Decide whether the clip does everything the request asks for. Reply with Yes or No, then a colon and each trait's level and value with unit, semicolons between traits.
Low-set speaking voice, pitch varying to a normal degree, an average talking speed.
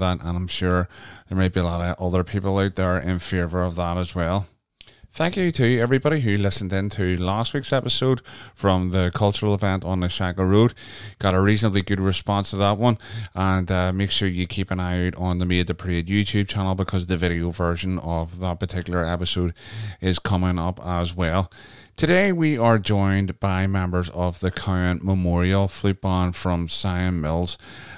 No: very low, 95 Hz; narrow, 2.2 semitones; average, 195 wpm